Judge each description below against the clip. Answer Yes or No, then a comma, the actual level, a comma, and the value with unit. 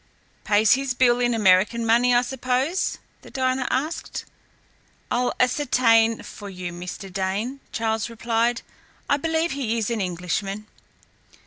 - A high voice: Yes, high, 235 Hz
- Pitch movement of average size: Yes, average, 3.7 semitones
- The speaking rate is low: Yes, slow, 130 wpm